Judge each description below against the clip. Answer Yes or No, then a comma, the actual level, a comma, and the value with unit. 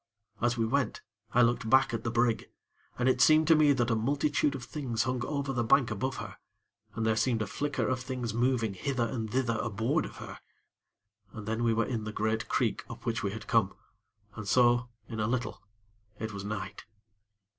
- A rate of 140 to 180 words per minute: No, fast, 205 wpm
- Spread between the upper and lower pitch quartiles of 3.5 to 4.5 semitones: No, average, 2.8 semitones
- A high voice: No, low, 120 Hz